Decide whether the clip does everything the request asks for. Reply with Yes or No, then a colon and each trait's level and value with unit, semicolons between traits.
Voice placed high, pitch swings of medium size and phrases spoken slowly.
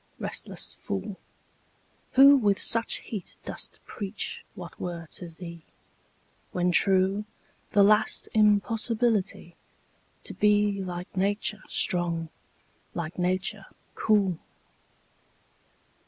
Yes: high, 195 Hz; average, 3.0 semitones; slow, 95 wpm